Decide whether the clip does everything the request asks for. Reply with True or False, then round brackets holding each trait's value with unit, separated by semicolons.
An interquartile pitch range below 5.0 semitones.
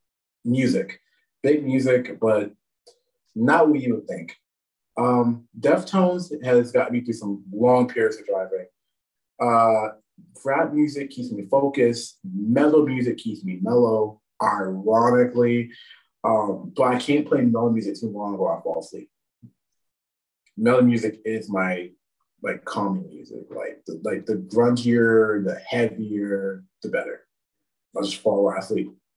False (5.3 semitones)